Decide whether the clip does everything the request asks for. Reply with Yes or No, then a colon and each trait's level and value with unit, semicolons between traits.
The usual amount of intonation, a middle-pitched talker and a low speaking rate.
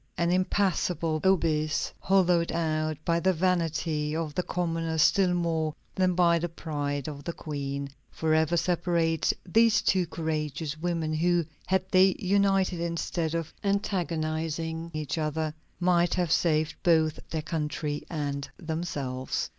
No: narrow, 2.2 semitones; medium, 165 Hz; slow, 130 wpm